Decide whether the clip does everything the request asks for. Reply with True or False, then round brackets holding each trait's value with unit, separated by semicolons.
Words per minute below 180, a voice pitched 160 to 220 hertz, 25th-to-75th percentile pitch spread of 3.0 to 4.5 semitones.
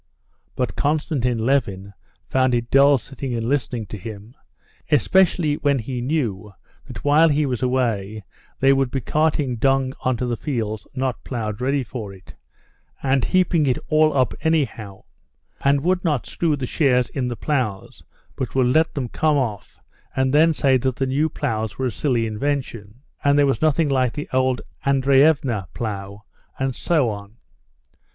False (165 wpm; 130 Hz; 3.8 semitones)